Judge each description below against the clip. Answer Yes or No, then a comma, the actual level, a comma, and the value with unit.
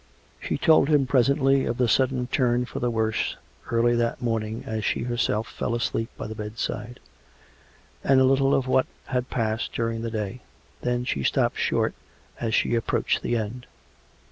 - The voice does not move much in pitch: Yes, narrow, 2.3 semitones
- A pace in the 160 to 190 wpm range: Yes, average, 175 wpm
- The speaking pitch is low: Yes, low, 120 Hz